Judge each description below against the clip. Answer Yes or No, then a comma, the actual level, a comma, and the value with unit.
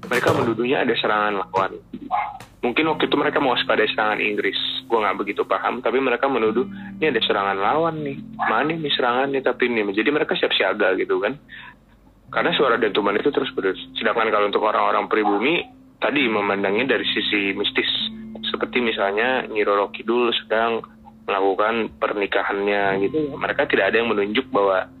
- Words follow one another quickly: Yes, fast, 160 wpm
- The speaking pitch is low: Yes, low, 115 Hz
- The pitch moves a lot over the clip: Yes, wide, 7.5 semitones